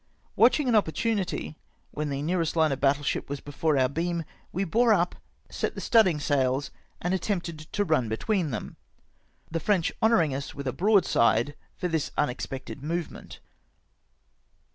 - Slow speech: No, average, 160 wpm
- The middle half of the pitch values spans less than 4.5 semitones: No, average, 5.0 semitones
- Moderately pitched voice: Yes, medium, 160 Hz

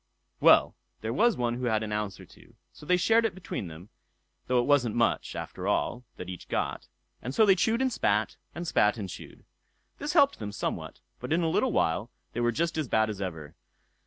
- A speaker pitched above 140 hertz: No, low, 120 Hz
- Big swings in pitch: Yes, wide, 8.9 semitones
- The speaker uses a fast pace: Yes, fast, 220 wpm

